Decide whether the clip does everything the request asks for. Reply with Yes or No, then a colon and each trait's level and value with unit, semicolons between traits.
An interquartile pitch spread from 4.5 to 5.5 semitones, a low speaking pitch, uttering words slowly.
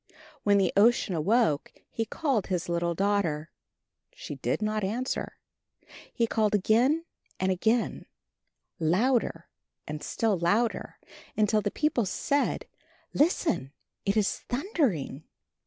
No: average, 5.1 semitones; high, 210 Hz; slow, 115 wpm